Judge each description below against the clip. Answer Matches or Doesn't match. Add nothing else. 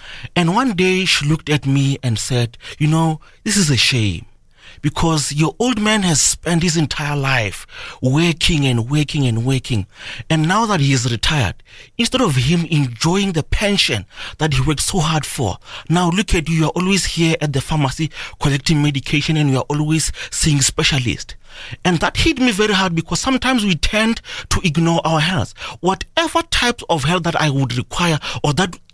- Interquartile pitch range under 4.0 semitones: Doesn't match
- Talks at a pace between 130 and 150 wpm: Doesn't match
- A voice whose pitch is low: Doesn't match